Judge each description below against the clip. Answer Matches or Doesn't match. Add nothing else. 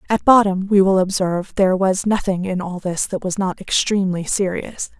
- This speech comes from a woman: Matches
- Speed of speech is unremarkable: Matches